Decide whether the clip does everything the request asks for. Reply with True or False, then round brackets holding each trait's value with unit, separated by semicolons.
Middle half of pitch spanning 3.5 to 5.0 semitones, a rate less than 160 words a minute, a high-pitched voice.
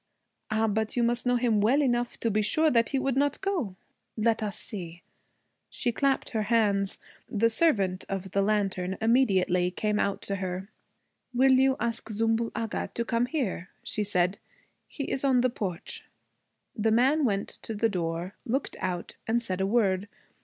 False (3.8 semitones; 175 wpm; 220 Hz)